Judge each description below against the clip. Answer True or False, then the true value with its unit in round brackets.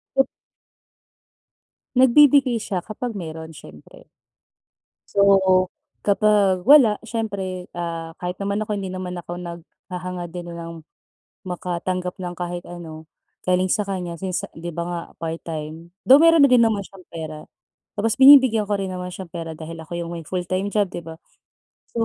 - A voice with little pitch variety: False (3.5 semitones)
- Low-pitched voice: False (180 Hz)